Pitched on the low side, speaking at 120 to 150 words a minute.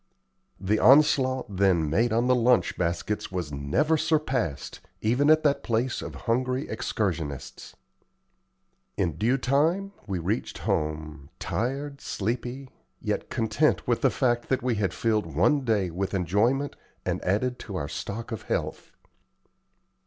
Yes: low, 115 Hz; average, 140 wpm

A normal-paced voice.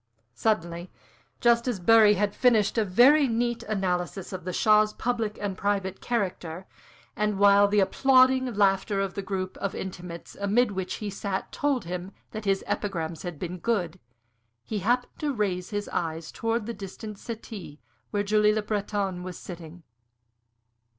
Yes: average, 155 wpm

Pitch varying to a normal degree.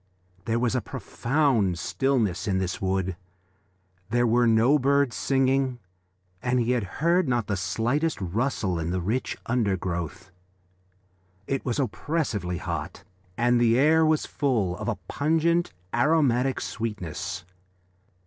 No: wide, 6.0 semitones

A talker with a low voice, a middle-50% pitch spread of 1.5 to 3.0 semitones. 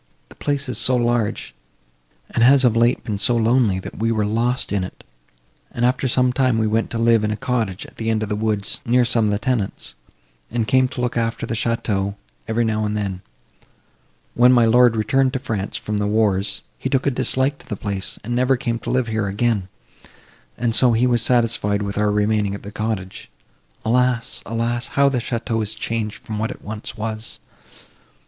Yes: low, 115 Hz; narrow, 2.6 semitones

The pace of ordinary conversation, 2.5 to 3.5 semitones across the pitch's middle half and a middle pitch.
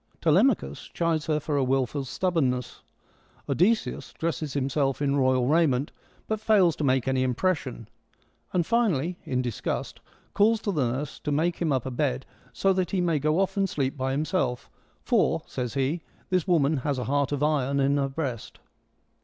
No: average, 175 wpm; average, 4.4 semitones; medium, 145 Hz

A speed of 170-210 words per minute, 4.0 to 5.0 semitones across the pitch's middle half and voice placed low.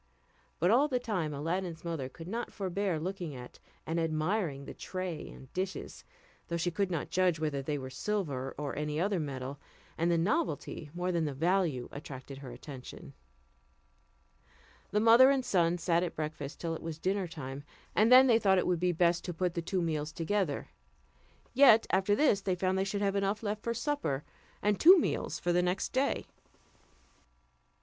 No: average, 185 wpm; average, 4.5 semitones; medium, 175 Hz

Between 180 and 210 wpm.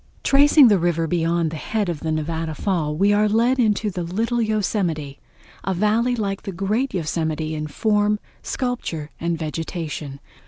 No: average, 160 wpm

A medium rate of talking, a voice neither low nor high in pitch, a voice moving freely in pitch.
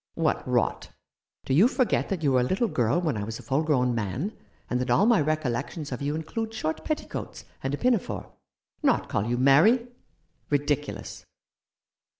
Yes: average, 180 wpm; medium, 145 Hz; wide, 7.5 semitones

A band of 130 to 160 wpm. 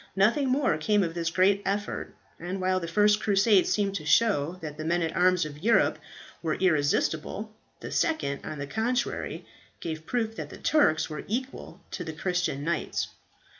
No: average, 175 wpm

